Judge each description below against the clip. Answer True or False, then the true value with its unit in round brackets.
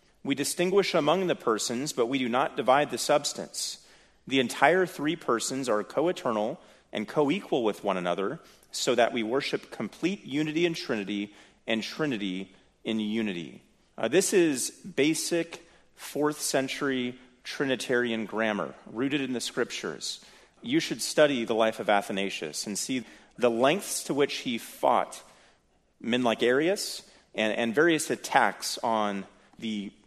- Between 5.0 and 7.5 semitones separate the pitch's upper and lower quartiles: True (5.6 semitones)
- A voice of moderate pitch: False (125 Hz)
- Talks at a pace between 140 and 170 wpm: True (145 wpm)